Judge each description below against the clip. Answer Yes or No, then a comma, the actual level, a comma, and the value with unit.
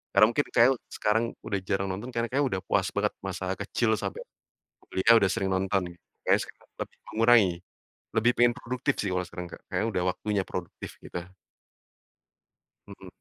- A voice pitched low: Yes, low, 105 Hz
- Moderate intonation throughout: Yes, average, 3.7 semitones